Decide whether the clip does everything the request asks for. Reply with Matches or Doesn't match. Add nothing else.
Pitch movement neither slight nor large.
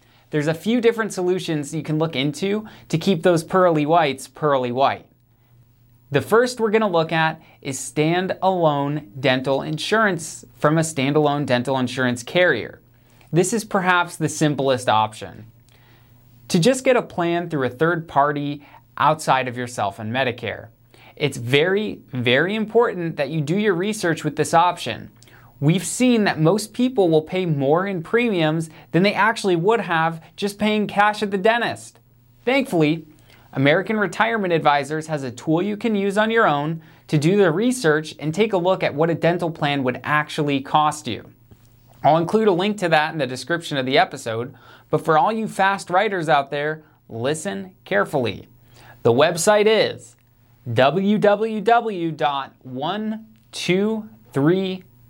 Doesn't match